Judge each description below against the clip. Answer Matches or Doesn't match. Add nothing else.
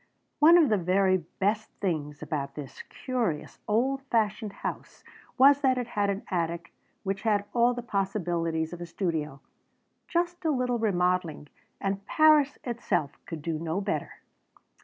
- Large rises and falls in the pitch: Matches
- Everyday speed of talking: Matches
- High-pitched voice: Matches